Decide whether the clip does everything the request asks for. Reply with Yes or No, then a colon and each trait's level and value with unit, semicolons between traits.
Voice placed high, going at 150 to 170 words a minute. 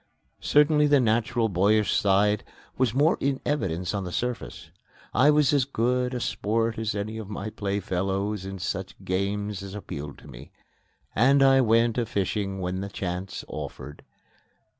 No: low, 105 Hz; average, 160 wpm